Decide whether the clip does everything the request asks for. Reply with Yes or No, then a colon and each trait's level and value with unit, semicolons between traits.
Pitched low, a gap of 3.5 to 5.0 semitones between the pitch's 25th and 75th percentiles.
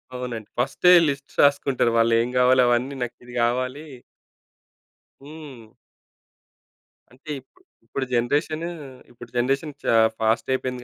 No: low, 125 Hz; average, 2.7 semitones